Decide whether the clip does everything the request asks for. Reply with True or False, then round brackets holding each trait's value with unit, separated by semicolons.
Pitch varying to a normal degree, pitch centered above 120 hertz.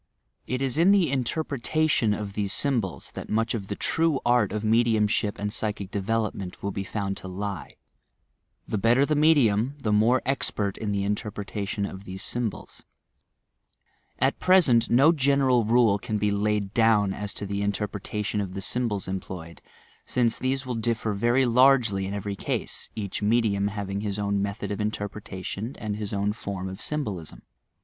False (3.2 semitones; 105 Hz)